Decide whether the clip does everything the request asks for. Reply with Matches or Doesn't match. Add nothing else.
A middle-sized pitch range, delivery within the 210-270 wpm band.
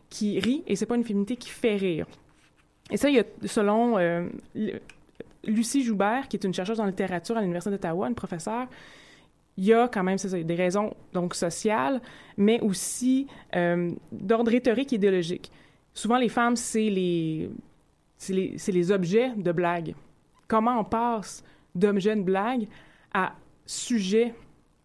Doesn't match